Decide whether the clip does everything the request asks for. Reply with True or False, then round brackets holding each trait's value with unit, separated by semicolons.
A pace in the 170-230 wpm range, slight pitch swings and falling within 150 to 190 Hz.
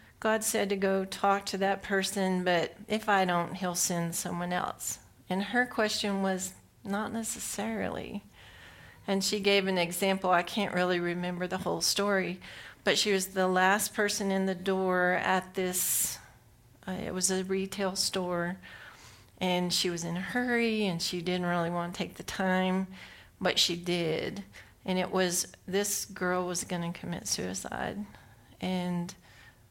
False (160 wpm; 2.0 semitones; 185 Hz)